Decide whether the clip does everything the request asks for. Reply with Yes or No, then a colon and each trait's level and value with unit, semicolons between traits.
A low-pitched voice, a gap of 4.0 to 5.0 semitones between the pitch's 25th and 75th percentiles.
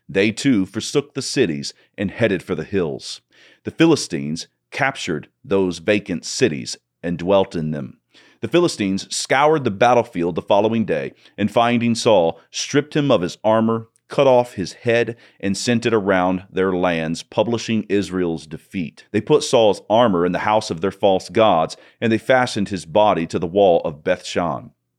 Yes: low, 105 Hz; average, 4.5 semitones